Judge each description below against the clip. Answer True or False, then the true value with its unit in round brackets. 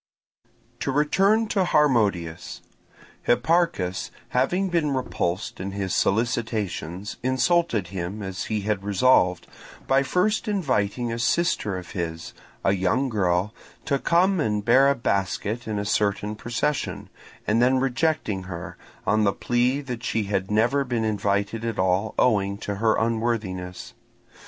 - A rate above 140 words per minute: False (135 wpm)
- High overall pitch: False (110 Hz)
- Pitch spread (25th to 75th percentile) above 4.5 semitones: True (5.1 semitones)